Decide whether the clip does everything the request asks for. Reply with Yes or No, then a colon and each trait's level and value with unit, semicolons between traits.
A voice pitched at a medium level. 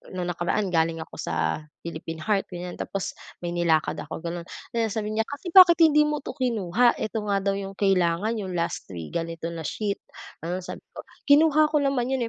No: high, 195 Hz